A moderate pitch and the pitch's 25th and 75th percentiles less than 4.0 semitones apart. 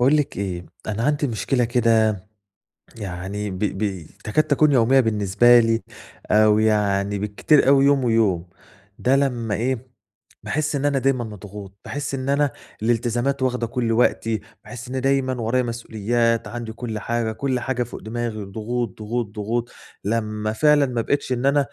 No: low, 115 Hz; average, 3.4 semitones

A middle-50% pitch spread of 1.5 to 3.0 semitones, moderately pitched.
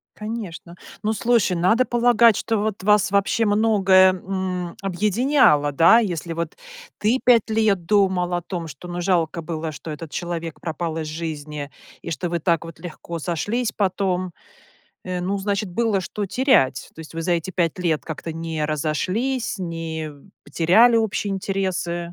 No: average, 4.0 semitones; medium, 180 Hz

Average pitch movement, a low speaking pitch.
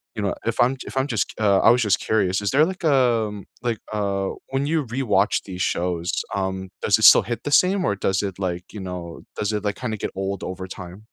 Yes: average, 4.2 semitones; low, 105 Hz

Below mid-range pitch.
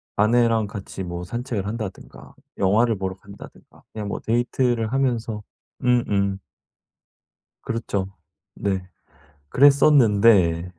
Yes: low, 110 Hz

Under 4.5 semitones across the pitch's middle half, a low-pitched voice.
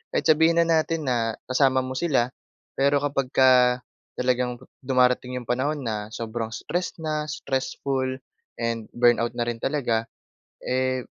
Yes: average, 2.9 semitones; low, 130 Hz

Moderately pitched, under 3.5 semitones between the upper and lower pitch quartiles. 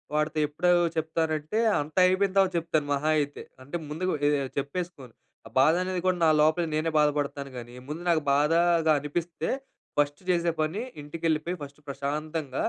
Yes: medium, 155 Hz; average, 2.8 semitones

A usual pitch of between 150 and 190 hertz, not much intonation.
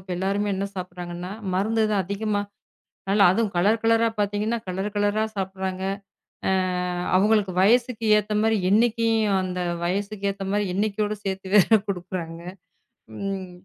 No: high, 200 Hz; narrow, 2.3 semitones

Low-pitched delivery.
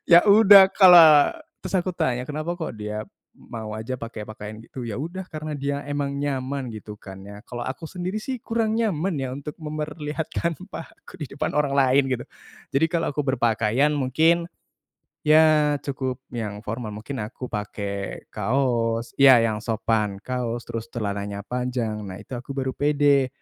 Yes: low, 130 Hz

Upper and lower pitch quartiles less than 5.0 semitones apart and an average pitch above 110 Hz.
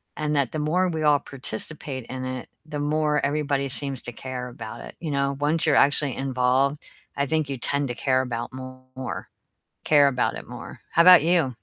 Yes: narrow, 2.6 semitones; medium, 140 Hz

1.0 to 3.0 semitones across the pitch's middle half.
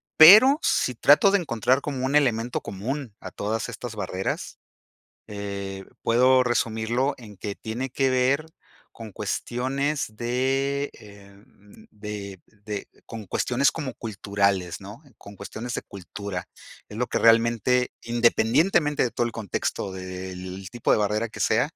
No: average, 4.2 semitones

